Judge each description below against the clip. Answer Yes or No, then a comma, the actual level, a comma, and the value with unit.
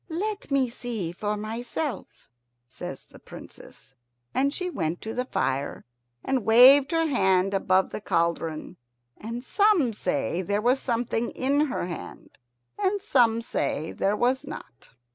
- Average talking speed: Yes, average, 145 wpm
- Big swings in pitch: Yes, wide, 6.3 semitones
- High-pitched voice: Yes, high, 235 Hz